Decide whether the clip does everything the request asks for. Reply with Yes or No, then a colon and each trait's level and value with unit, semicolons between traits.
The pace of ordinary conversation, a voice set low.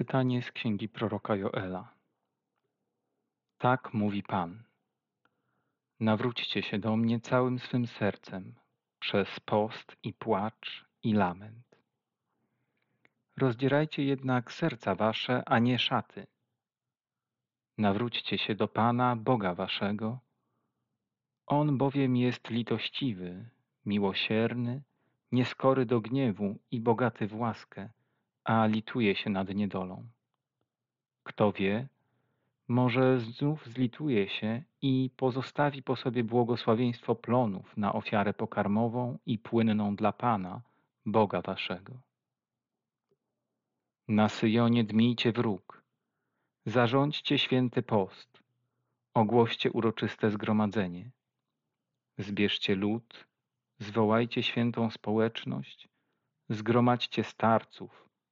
No: slow, 90 wpm; low, 120 Hz